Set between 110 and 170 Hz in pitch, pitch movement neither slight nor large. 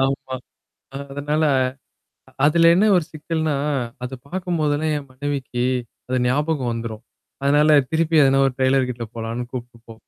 Yes: medium, 140 Hz; average, 3.6 semitones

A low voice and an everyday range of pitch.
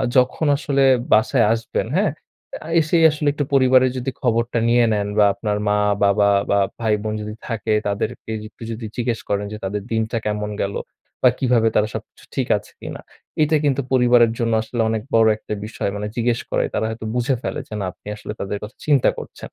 Yes: low, 115 Hz; average, 3.2 semitones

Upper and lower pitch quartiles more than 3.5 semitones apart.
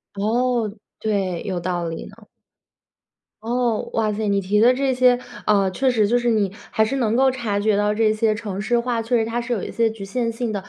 No: average, 2.9 semitones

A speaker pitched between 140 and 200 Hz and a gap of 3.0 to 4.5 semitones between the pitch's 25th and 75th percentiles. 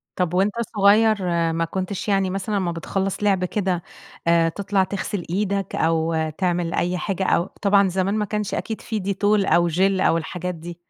No: high, 190 Hz; narrow, 2.6 semitones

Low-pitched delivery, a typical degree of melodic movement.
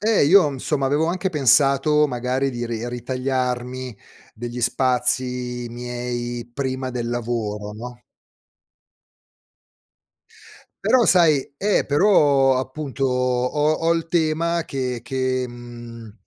Yes: low, 130 Hz; average, 3.3 semitones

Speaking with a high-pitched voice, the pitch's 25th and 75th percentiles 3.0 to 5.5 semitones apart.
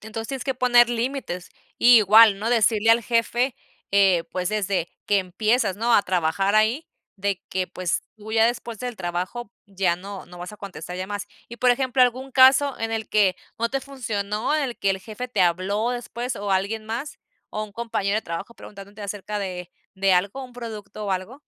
Yes: high, 215 Hz; average, 3.7 semitones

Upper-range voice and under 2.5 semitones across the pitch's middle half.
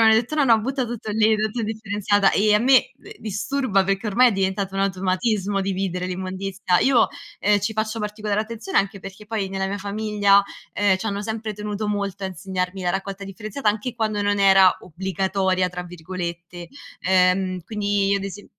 Yes: high, 200 Hz; narrow, 2.1 semitones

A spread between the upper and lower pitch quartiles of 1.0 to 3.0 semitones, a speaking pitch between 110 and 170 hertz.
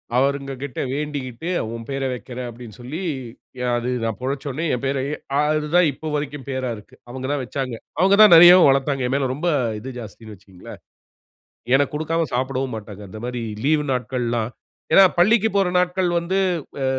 No: average, 3.8 semitones; low, 135 Hz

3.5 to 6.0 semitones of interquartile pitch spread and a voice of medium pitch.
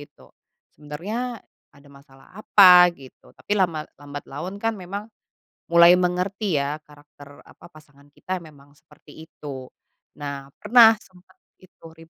Yes: average, 4.5 semitones; medium, 155 Hz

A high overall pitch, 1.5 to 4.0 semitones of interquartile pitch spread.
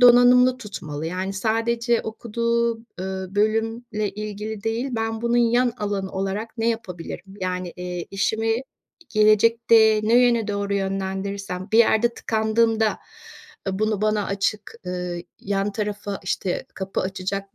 Yes: high, 215 Hz; average, 2.9 semitones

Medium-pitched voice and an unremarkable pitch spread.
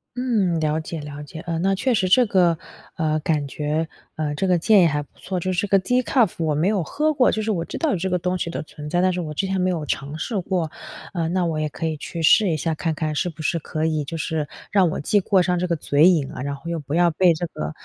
Yes: medium, 170 Hz; average, 3.3 semitones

